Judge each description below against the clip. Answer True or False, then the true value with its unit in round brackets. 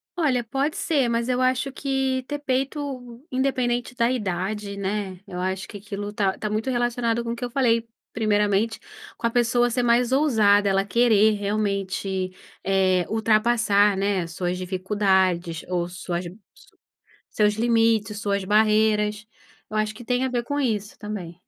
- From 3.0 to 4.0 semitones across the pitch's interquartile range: True (3.4 semitones)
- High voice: True (215 Hz)